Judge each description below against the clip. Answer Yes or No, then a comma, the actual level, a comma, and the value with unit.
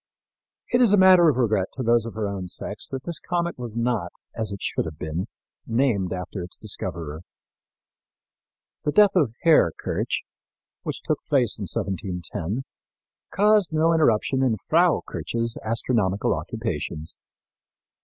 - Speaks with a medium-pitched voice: No, low, 115 Hz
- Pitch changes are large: Yes, wide, 8.5 semitones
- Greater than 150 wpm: No, average, 145 wpm